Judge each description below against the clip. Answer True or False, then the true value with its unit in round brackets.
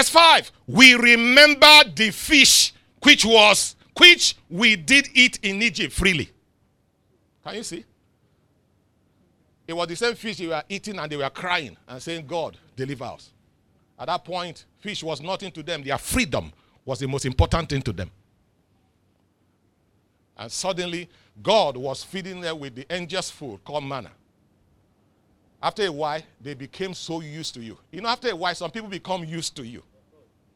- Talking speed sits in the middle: True (165 wpm)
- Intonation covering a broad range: True (8.7 semitones)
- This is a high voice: False (165 Hz)